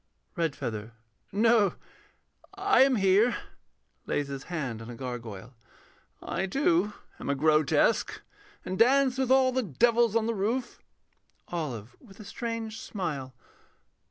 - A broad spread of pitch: Yes, wide, 8.9 semitones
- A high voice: Yes, high, 195 Hz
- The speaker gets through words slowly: Yes, slow, 130 wpm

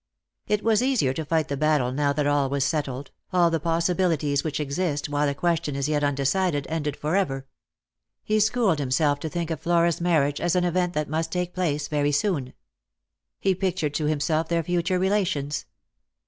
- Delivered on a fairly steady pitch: No, average, 3.6 semitones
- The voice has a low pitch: No, medium, 155 Hz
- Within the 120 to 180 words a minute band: No, average, 190 wpm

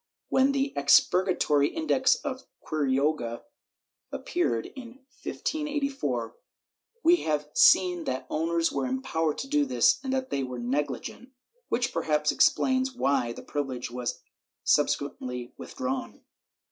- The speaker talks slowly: Yes, slow, 130 wpm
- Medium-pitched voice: Yes, medium, 165 Hz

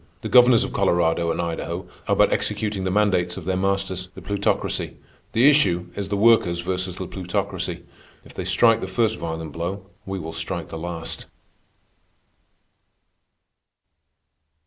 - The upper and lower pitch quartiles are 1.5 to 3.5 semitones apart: Yes, average, 2.9 semitones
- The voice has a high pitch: No, very low, 95 Hz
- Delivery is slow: No, average, 145 wpm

